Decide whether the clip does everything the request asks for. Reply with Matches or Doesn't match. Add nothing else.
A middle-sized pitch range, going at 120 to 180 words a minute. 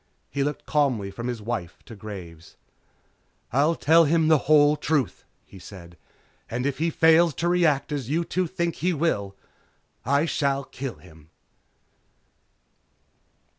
Doesn't match